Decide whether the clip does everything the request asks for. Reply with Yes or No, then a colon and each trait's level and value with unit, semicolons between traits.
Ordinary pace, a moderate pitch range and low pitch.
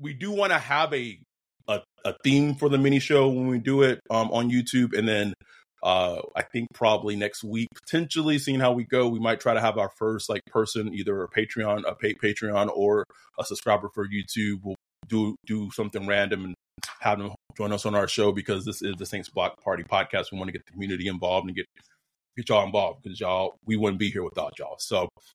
No: fast, 225 wpm; average, 3.5 semitones; low, 105 Hz